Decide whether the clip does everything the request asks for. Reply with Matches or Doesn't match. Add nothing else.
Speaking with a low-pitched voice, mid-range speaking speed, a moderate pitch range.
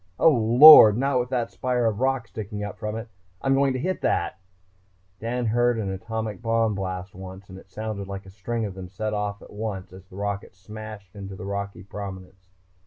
Doesn't match